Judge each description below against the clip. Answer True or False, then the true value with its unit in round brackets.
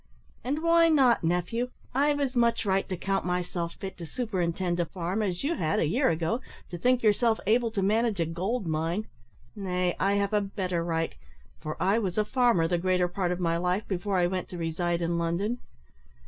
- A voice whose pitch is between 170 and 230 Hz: True (190 Hz)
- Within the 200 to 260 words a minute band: True (205 wpm)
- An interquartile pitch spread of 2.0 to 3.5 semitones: False (4.7 semitones)